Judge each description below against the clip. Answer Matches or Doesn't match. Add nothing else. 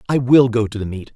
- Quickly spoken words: Matches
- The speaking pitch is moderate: Doesn't match